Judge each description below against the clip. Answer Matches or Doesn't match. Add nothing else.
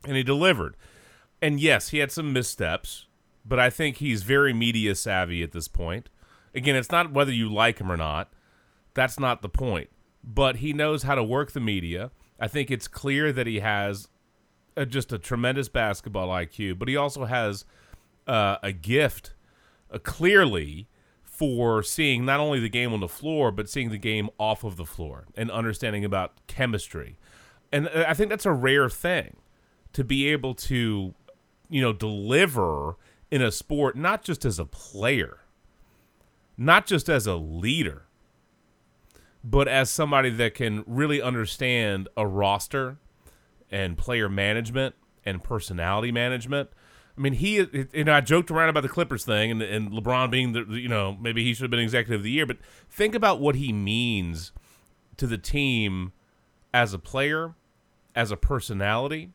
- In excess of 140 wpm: Matches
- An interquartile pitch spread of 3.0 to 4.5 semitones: Doesn't match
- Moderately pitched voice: Doesn't match